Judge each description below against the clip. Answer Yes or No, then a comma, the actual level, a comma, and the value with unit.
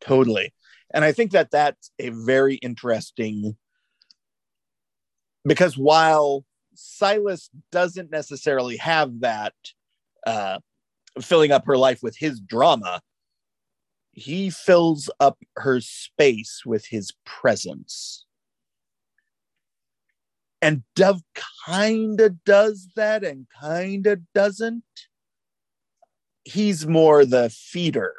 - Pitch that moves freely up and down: Yes, wide, 6.9 semitones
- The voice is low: No, medium, 155 Hz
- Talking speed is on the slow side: Yes, slow, 100 wpm